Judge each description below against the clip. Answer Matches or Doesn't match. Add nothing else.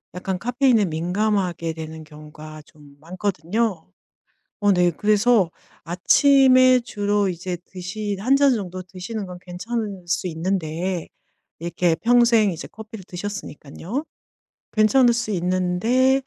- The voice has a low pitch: Doesn't match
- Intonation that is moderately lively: Matches